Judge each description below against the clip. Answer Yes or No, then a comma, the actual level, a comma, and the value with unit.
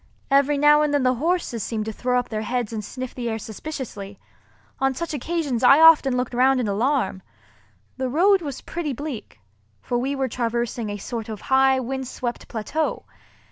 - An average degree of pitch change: Yes, average, 3.7 semitones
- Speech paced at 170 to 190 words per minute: Yes, average, 180 wpm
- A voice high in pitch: Yes, very high, 255 Hz